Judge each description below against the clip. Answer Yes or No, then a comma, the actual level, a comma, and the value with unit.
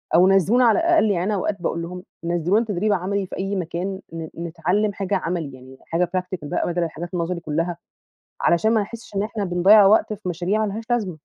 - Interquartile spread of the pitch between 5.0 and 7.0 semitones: No, average, 3.3 semitones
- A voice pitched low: No, medium, 185 Hz